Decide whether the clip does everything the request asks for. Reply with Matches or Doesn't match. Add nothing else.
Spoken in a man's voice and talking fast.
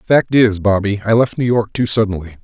Matches